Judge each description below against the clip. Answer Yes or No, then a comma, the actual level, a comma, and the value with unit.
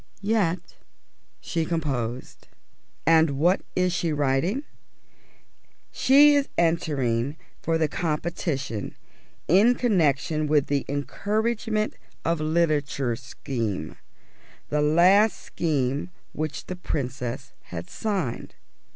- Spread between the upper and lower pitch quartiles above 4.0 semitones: Yes, average, 4.8 semitones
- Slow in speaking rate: Yes, slow, 95 wpm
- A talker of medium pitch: Yes, medium, 155 Hz